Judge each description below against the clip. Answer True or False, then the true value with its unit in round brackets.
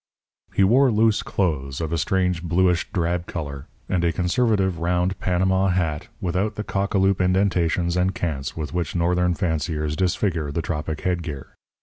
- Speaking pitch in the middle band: False (90 Hz)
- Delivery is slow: False (165 wpm)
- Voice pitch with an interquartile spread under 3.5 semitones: True (2.4 semitones)